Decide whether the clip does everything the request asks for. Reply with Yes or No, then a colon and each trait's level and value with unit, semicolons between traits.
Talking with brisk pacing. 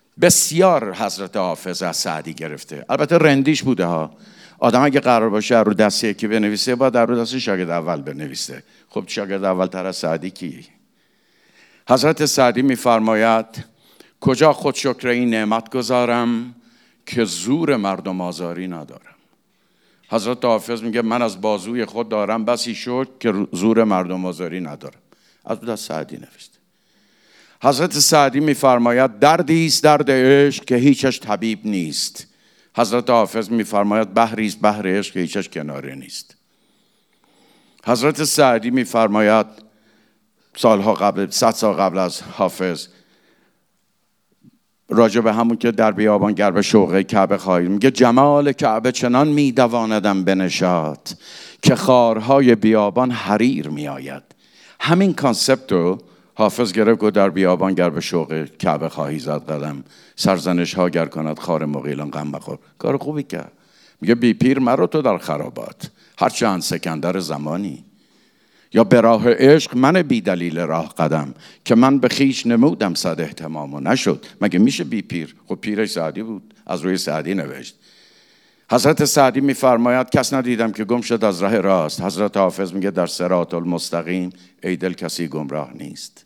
No: average, 145 wpm